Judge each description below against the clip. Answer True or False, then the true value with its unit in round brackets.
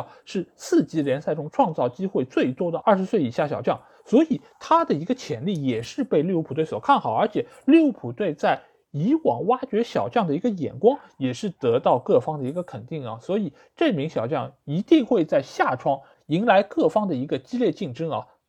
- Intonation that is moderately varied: False (8.7 semitones)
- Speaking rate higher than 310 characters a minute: False (300 characters per minute)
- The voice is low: False (205 Hz)